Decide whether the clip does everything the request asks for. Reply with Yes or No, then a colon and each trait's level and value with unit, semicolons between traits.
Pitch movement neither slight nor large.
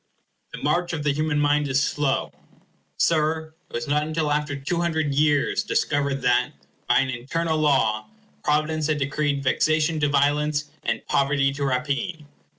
No: narrow, 1.9 semitones